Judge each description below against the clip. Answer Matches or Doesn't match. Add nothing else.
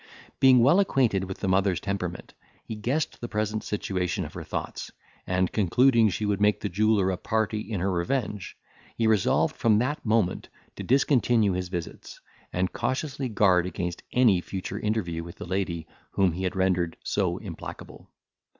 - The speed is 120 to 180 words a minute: Matches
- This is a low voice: Matches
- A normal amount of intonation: Matches